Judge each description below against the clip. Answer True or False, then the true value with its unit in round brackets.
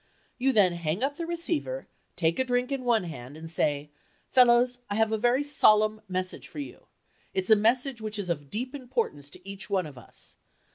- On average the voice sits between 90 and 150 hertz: False (220 Hz)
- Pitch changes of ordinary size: False (6.3 semitones)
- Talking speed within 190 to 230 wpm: True (200 wpm)